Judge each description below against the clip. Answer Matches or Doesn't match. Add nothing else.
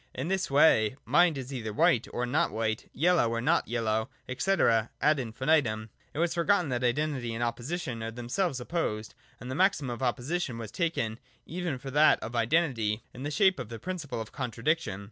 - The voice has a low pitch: Matches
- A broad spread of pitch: Matches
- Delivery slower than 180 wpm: Doesn't match